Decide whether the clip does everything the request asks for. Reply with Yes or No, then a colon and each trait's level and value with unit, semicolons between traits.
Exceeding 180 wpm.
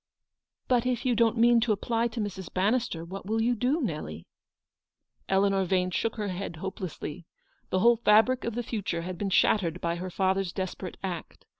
Yes: average, 190 wpm